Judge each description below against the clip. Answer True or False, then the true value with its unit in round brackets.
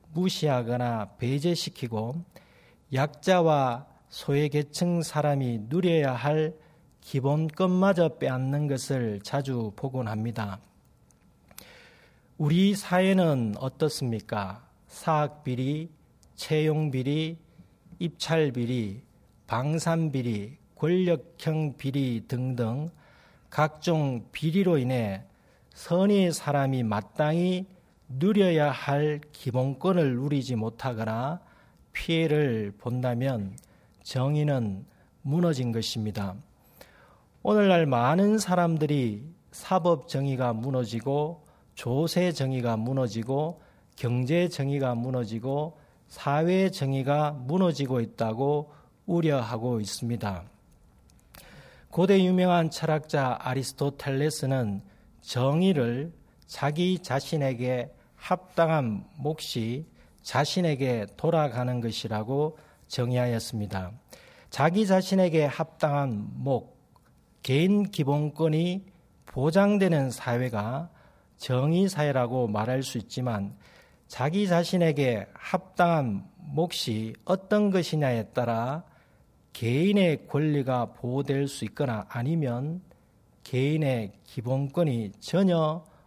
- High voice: False (140 Hz)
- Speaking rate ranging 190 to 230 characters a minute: True (215 characters per minute)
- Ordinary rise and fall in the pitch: True (4.9 semitones)